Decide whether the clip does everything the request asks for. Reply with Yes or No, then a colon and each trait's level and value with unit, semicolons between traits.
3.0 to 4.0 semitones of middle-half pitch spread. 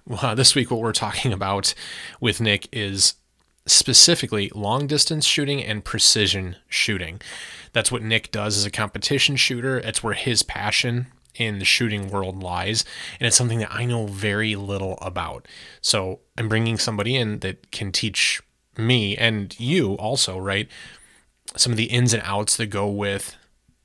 Yes: average, 3.4 semitones